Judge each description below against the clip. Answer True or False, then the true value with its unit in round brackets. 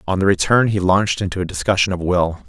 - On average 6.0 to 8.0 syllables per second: True (6.5 syllables/s)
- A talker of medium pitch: False (95 Hz)